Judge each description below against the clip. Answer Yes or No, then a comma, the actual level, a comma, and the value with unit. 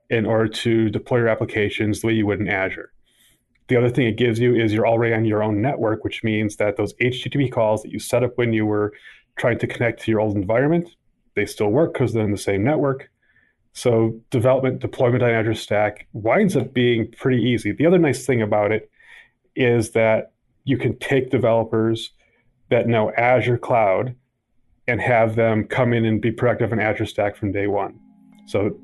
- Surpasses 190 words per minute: Yes, average, 200 wpm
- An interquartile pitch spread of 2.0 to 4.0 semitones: Yes, narrow, 2.4 semitones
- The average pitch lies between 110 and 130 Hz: Yes, low, 115 Hz